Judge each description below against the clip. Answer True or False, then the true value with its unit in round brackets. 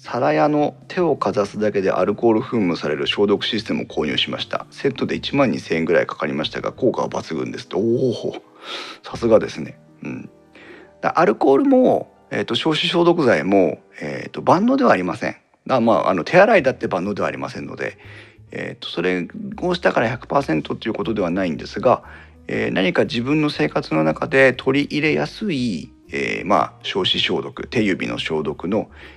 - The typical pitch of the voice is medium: False (125 Hz)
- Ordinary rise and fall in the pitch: False (8.1 semitones)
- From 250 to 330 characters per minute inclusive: False (370 characters per minute)